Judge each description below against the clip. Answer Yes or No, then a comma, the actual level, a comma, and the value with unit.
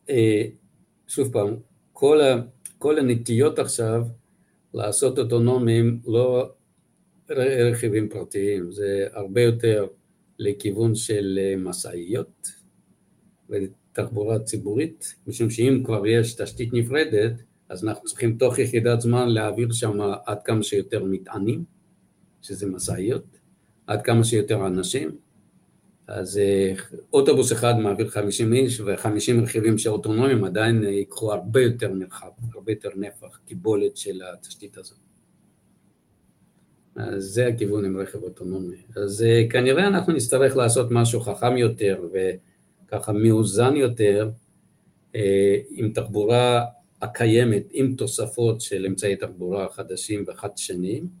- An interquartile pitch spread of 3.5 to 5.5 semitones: No, average, 2.8 semitones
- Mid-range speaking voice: No, low, 110 Hz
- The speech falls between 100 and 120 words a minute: Yes, average, 110 wpm